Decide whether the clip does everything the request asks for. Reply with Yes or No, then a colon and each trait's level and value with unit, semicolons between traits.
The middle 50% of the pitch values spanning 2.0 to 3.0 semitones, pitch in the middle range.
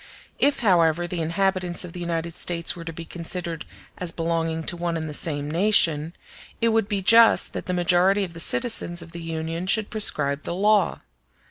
Yes: average, 2.7 semitones; medium, 170 Hz